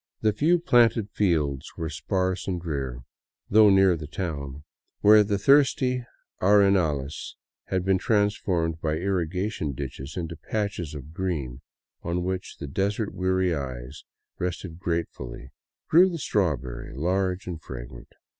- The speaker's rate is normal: No, slow, 125 wpm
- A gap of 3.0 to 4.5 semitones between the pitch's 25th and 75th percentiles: No, average, 5.3 semitones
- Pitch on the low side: Yes, very low, 90 Hz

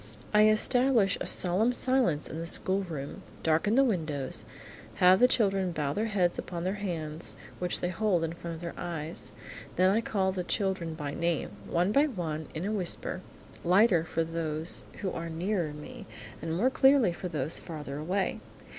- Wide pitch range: No, average, 4.0 semitones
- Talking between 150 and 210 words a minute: Yes, average, 175 wpm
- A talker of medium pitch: Yes, medium, 180 Hz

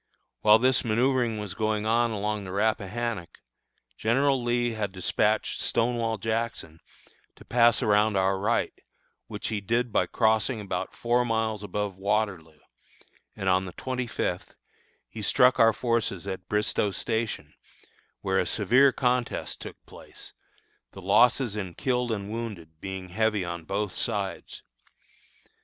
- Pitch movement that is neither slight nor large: Yes, average, 3.2 semitones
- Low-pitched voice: Yes, low, 110 Hz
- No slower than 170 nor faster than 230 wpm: No, average, 140 wpm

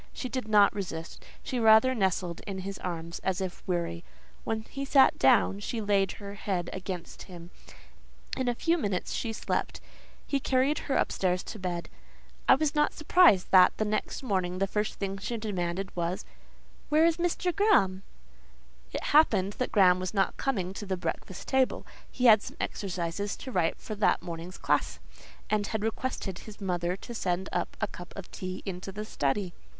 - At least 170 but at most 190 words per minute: Yes, average, 175 wpm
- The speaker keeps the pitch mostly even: No, average, 4.1 semitones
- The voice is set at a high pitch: Yes, high, 195 Hz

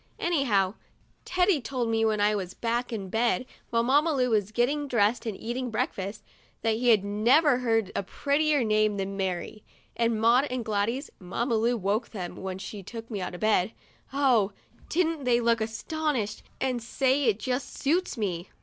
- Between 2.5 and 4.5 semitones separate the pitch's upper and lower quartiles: Yes, average, 3.8 semitones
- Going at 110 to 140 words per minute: No, average, 175 wpm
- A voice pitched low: No, high, 230 Hz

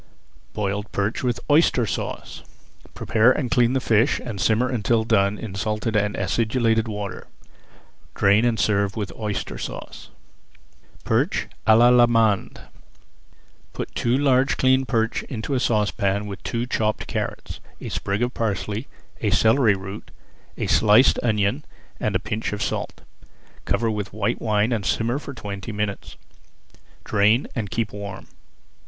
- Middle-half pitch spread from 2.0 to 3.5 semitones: Yes, narrow, 2.6 semitones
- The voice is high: No, low, 110 Hz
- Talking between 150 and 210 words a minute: No, average, 140 wpm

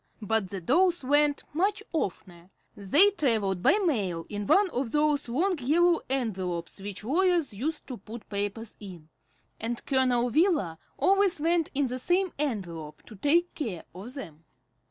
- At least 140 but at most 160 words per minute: Yes, average, 155 wpm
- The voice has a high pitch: Yes, very high, 250 Hz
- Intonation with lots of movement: Yes, wide, 8.4 semitones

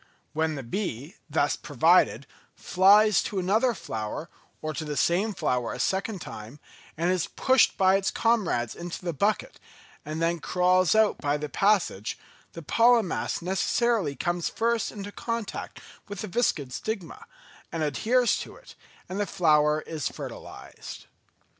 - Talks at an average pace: Yes, average, 150 wpm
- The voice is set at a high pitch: No, medium, 180 Hz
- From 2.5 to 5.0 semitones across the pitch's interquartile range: No, wide, 5.6 semitones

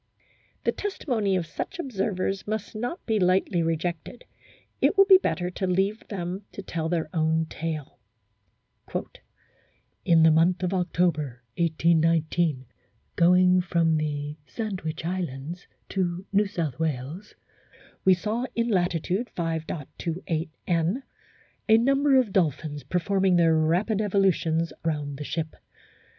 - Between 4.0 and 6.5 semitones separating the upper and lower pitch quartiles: No, average, 3.5 semitones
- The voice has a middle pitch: Yes, medium, 175 Hz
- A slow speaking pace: Yes, slow, 125 wpm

